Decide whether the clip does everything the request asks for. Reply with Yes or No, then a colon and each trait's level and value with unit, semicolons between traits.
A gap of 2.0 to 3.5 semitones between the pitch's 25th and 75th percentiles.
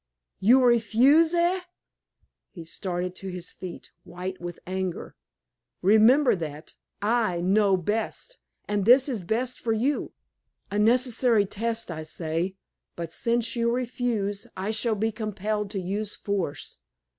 No: average, 4.3 semitones